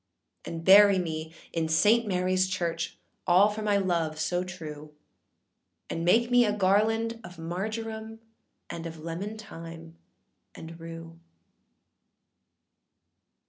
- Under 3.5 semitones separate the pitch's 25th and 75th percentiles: No, average, 4.1 semitones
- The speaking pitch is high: No, medium, 180 Hz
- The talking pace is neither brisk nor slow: No, slow, 115 wpm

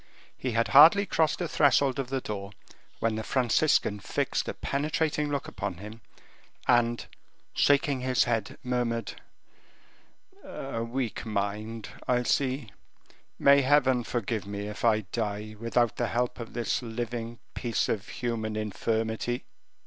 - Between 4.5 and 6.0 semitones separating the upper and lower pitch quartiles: No, average, 3.1 semitones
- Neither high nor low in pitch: No, low, 120 Hz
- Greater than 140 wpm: No, slow, 135 wpm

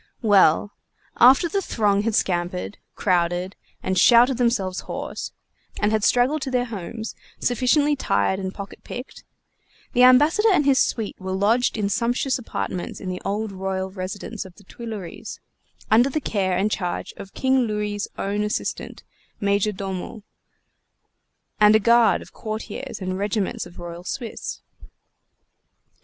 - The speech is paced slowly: No, average, 145 wpm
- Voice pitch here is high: Yes, high, 210 Hz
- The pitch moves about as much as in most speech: Yes, average, 4.3 semitones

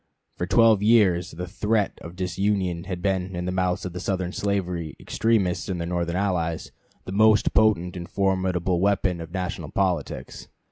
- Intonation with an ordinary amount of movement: No, narrow, 2.2 semitones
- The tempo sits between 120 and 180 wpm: Yes, average, 170 wpm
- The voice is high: No, very low, 90 Hz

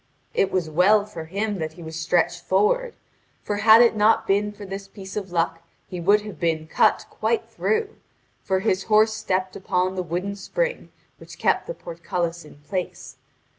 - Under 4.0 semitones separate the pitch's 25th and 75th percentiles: Yes, average, 3.5 semitones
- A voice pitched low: No, high, 195 Hz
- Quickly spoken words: No, average, 180 wpm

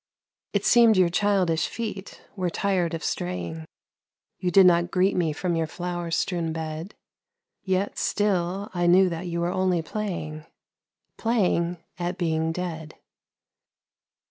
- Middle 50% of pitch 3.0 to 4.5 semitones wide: No, narrow, 2.6 semitones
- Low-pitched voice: No, medium, 175 Hz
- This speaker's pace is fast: No, slow, 135 wpm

